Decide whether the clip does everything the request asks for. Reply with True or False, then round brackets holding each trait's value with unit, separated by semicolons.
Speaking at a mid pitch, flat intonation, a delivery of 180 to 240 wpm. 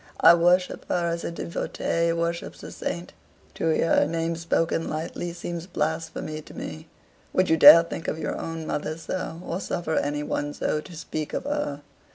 True (165 Hz; 1.5 semitones; 185 wpm)